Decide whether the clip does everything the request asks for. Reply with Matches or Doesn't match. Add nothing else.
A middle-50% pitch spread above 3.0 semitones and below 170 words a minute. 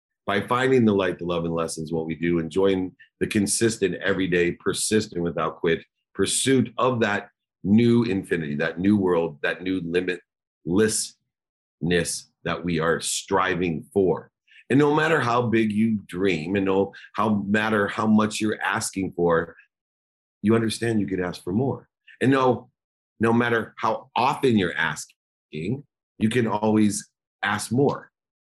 Matches